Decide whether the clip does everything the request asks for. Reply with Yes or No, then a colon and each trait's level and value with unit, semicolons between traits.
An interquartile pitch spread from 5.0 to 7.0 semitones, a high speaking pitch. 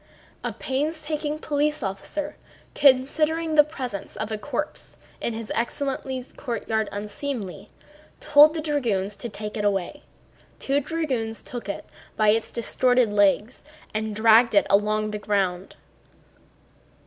Yes: wide, 5.6 semitones; high, 235 Hz